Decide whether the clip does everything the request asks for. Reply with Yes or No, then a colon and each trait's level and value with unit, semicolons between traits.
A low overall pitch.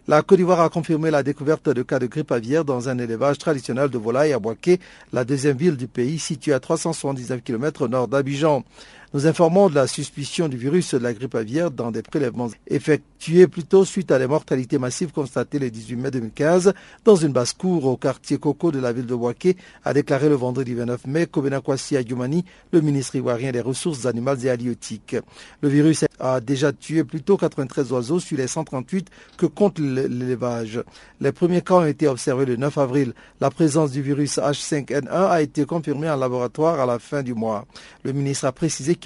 No: medium, 145 Hz